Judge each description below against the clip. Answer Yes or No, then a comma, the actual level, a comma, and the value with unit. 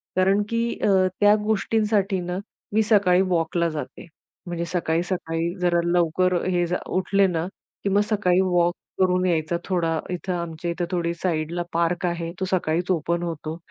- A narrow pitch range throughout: Yes, narrow, 1.9 semitones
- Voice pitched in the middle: Yes, medium, 175 Hz